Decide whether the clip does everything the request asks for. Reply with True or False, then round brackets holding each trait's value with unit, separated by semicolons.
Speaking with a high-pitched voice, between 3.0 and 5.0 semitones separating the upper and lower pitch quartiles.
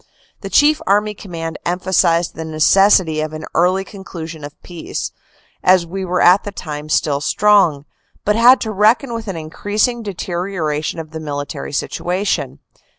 False (180 Hz; 4.4 semitones)